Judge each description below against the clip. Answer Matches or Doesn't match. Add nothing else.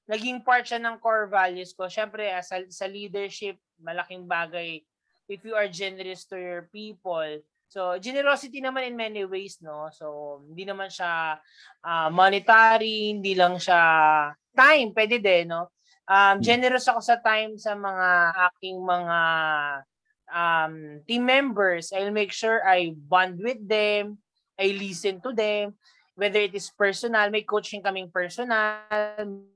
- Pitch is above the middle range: Matches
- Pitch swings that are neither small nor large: Matches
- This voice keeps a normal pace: Matches